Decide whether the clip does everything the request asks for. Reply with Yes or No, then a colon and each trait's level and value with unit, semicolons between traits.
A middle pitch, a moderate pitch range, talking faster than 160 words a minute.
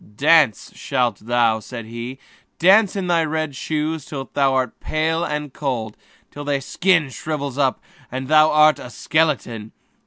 No: medium, 145 Hz; average, 3.8 semitones; average, 155 wpm